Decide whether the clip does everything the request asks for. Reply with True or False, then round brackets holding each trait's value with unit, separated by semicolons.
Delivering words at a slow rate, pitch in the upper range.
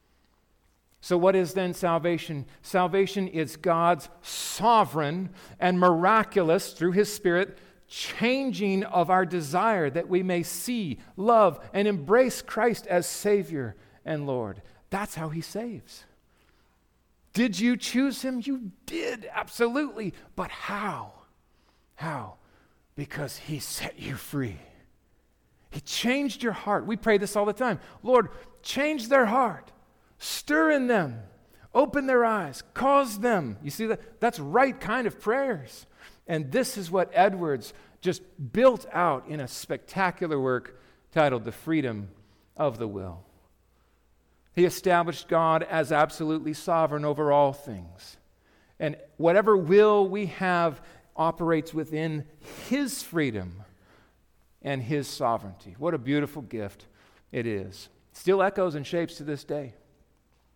False (130 wpm; 170 Hz)